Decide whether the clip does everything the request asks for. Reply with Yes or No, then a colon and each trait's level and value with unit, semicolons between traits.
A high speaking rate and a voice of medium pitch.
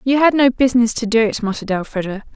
No: fast, 230 wpm; high, 235 Hz